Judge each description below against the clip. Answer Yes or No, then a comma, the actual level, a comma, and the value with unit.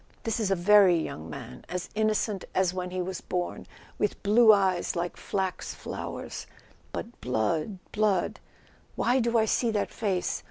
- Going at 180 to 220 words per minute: No, average, 160 wpm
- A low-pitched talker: No, high, 190 Hz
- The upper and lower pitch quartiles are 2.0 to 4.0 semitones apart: Yes, average, 3.3 semitones